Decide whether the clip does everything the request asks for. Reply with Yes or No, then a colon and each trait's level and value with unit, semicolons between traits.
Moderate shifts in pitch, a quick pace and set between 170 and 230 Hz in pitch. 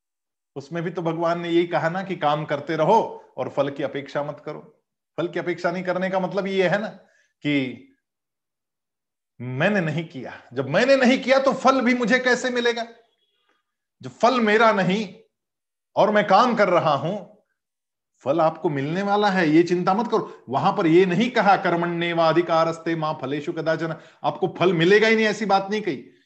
No: average, 4.8 semitones; average, 180 wpm; medium, 185 Hz